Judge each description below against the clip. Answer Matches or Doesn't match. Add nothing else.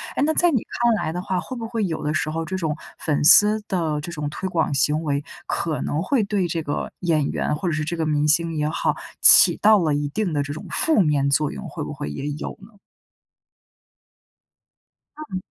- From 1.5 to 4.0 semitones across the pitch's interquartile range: Doesn't match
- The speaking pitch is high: Doesn't match